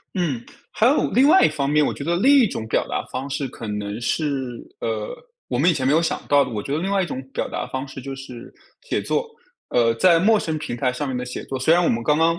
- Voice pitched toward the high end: No, medium, 140 Hz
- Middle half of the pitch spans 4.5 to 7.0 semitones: Yes, average, 5.2 semitones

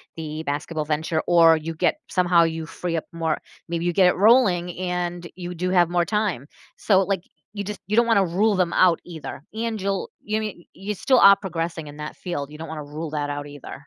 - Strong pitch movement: No, average, 3.3 semitones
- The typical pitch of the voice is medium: Yes, medium, 175 Hz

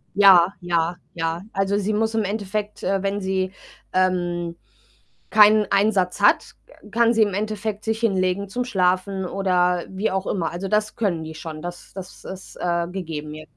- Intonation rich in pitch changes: No, average, 2.9 semitones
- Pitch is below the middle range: No, high, 190 Hz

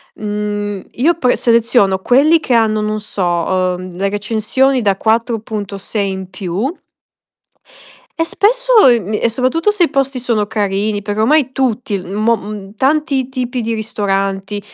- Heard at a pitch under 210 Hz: No, high, 220 Hz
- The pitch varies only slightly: No, average, 4.1 semitones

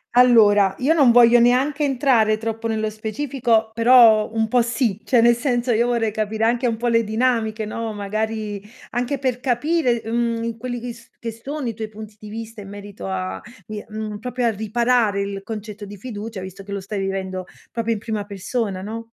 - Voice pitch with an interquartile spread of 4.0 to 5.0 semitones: No, narrow, 2.4 semitones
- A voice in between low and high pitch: No, high, 225 Hz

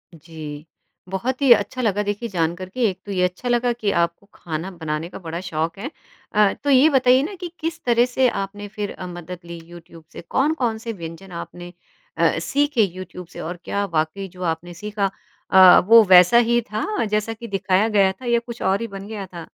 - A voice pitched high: Yes, high, 195 Hz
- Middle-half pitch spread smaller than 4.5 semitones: No, average, 5.0 semitones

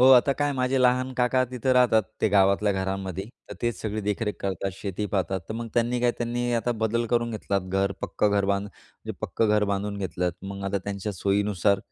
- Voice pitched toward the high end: No, low, 105 Hz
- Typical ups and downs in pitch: Yes, average, 3.5 semitones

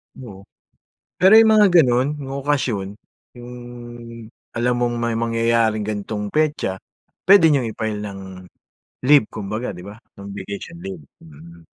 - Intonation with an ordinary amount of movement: No, wide, 5.8 semitones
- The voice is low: Yes, low, 115 Hz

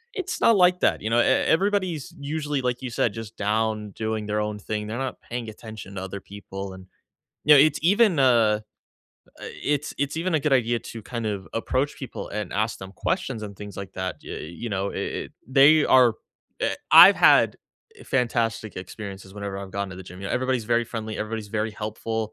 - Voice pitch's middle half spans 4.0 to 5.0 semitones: Yes, average, 4.6 semitones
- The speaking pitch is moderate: No, low, 110 Hz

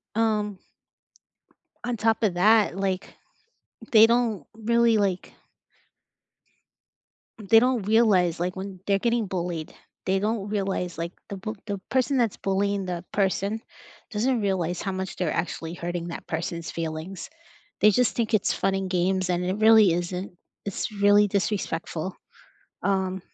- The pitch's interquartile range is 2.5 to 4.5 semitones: Yes, average, 3.2 semitones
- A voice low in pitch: No, high, 195 Hz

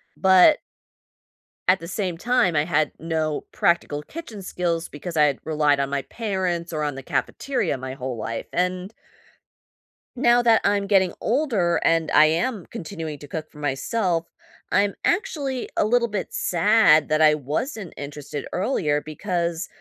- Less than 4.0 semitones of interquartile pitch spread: No, wide, 5.4 semitones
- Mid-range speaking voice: Yes, medium, 170 Hz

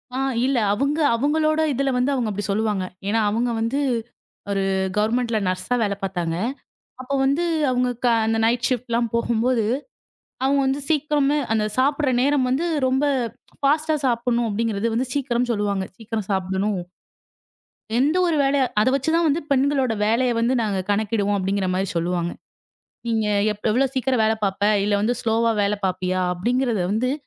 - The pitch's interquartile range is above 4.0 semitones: Yes, average, 4.5 semitones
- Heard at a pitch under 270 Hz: Yes, high, 235 Hz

